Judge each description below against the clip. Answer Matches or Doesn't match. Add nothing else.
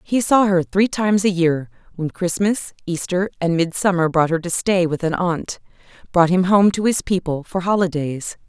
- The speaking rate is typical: Matches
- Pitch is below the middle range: Doesn't match